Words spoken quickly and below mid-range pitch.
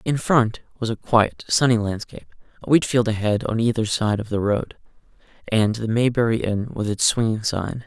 No: average, 190 wpm; low, 110 Hz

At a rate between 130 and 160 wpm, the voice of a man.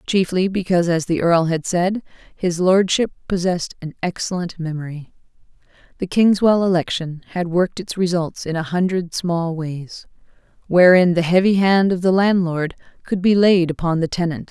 No: average, 155 wpm; female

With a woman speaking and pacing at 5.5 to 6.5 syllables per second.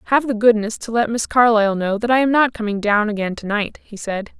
Yes: female; 5.9 syllables/s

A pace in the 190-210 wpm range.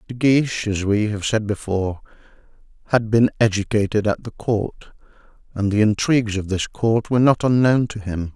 No: average, 170 wpm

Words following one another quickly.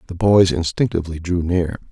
No: average, 155 wpm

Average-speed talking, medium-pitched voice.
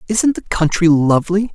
Yes: average, 155 wpm; medium, 180 Hz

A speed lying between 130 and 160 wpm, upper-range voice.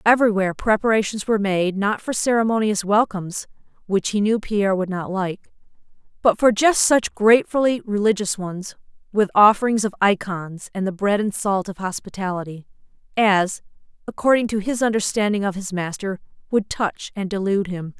Yes: average, 155 wpm; high, 205 Hz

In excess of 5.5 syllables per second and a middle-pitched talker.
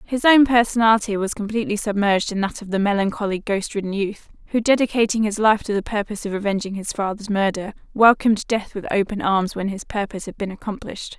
No: 6.3 syllables/s; high, 210 Hz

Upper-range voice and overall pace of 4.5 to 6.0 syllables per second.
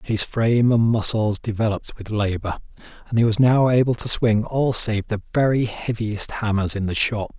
No: low, 110 Hz; 5.1 syllables/s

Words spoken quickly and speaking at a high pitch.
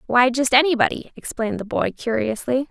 No: average, 155 wpm; very high, 250 Hz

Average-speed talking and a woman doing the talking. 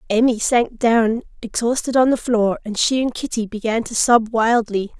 Yes: average, 180 wpm; female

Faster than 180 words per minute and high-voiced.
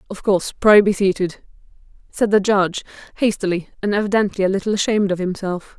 No: average, 165 wpm; high, 195 Hz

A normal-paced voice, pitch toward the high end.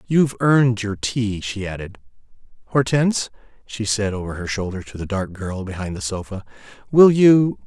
No: average, 165 wpm; low, 110 Hz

